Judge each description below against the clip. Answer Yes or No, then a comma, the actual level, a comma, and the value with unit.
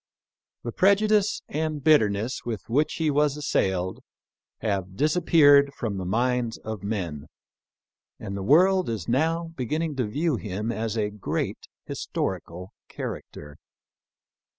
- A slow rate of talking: Yes, slow, 130 wpm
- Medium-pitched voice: No, low, 120 Hz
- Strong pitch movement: Yes, wide, 7.1 semitones